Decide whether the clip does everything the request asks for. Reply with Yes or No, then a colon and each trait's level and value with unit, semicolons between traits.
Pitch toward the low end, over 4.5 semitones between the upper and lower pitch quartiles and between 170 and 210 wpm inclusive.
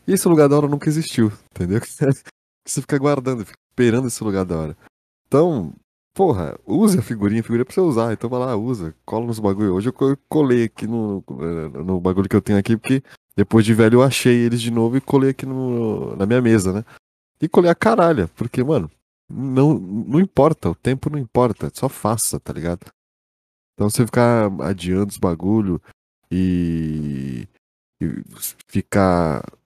Yes: low, 115 Hz; average, 5.2 semitones; average, 180 wpm